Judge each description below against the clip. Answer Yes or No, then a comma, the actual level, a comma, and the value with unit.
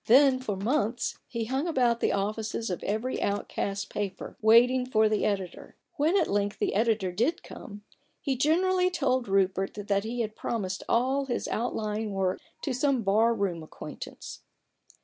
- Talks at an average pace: Yes, average, 160 wpm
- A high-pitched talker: Yes, high, 225 Hz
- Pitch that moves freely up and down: No, average, 4.3 semitones